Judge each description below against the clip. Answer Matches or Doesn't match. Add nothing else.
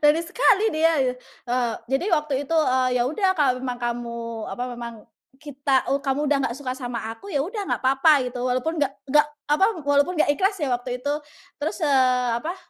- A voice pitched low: Doesn't match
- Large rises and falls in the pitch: Doesn't match